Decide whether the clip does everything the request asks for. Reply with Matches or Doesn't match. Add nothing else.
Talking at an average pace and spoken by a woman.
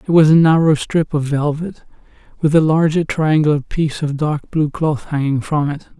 Doesn't match